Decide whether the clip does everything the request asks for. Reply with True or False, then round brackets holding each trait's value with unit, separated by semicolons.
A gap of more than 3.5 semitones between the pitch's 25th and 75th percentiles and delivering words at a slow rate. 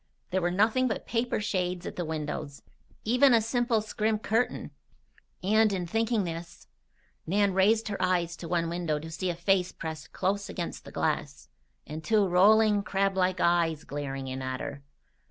False (4.4 semitones; 170 wpm)